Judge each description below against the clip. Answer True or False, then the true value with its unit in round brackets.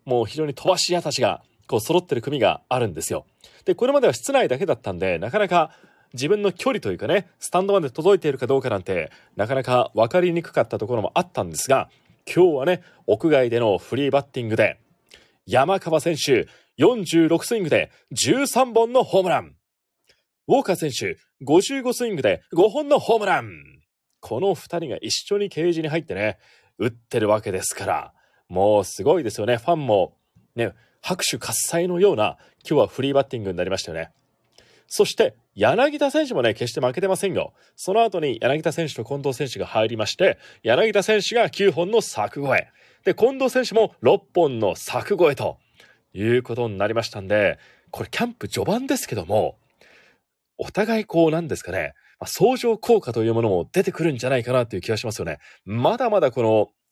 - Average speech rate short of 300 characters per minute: False (350 characters per minute)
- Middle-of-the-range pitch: True (170 Hz)